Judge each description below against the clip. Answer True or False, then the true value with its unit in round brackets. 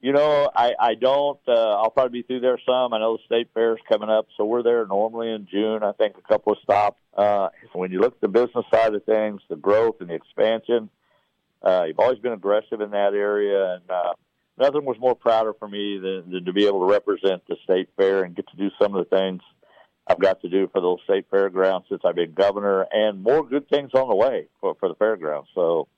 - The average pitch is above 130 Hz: False (110 Hz)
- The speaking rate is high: True (245 wpm)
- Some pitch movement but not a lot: True (4.0 semitones)